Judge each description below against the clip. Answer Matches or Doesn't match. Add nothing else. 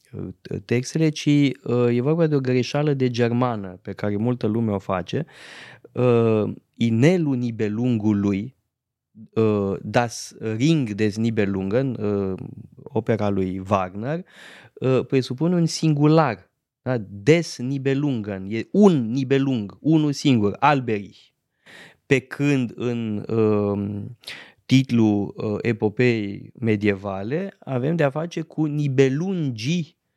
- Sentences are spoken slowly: Matches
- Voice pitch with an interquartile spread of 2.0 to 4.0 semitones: Doesn't match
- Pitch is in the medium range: Doesn't match